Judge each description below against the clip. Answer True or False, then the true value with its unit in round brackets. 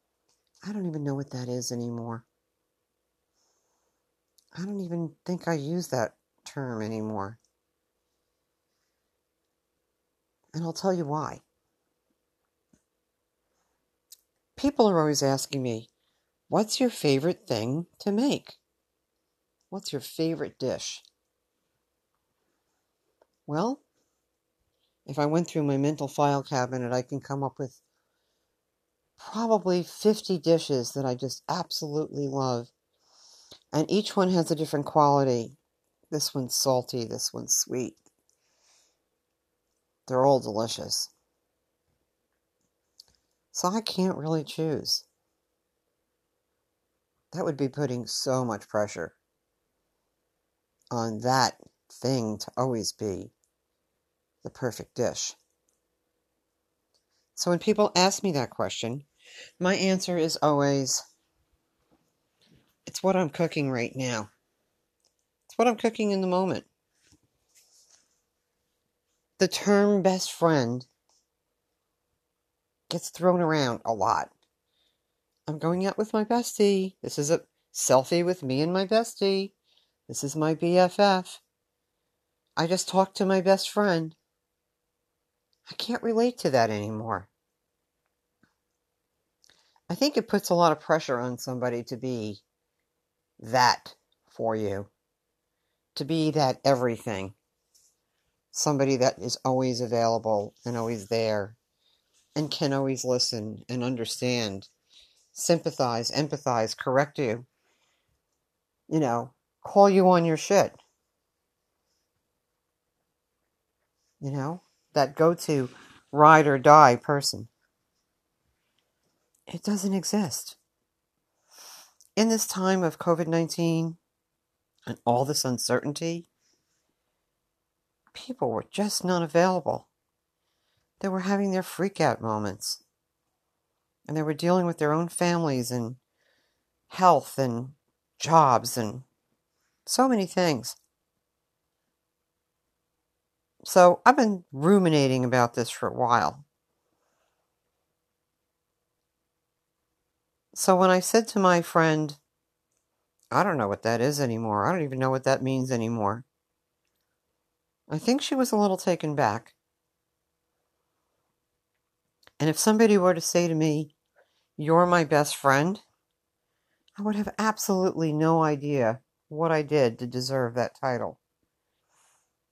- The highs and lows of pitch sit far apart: True (6.2 semitones)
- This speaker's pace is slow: True (110 wpm)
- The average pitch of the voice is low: False (150 Hz)